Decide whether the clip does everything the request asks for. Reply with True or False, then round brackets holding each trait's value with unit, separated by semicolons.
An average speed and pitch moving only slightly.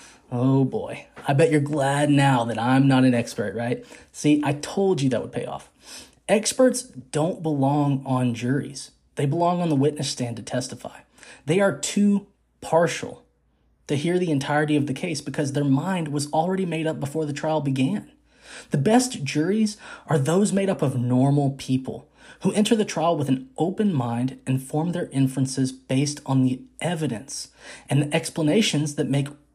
False (175 wpm; 3.6 semitones)